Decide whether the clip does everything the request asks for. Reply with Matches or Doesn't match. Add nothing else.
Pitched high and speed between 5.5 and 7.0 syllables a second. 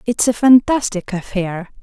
Doesn't match